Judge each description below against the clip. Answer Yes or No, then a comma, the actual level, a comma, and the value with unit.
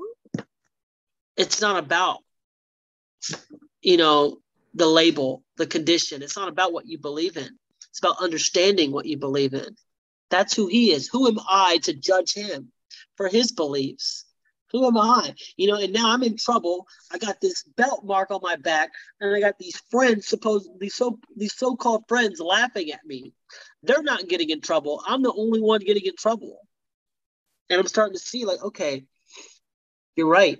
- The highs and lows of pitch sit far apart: Yes, wide, 5.8 semitones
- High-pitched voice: Yes, high, 200 Hz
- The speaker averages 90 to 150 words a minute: No, average, 175 wpm